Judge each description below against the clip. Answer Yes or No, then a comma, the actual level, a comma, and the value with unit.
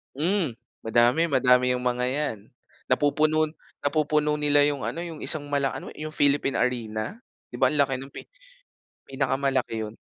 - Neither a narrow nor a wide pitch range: Yes, average, 3.2 semitones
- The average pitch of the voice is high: No, medium, 140 Hz